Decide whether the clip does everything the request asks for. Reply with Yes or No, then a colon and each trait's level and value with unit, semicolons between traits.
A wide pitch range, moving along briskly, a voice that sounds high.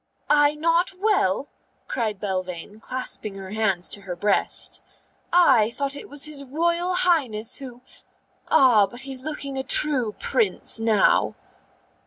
No: wide, 6.1 semitones; slow, 135 wpm; very high, 255 Hz